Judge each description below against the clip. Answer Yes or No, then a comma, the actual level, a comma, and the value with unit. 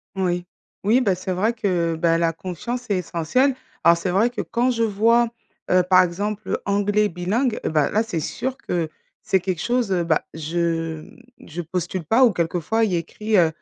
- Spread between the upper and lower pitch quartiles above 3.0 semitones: Yes, average, 4.7 semitones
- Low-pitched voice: No, medium, 185 Hz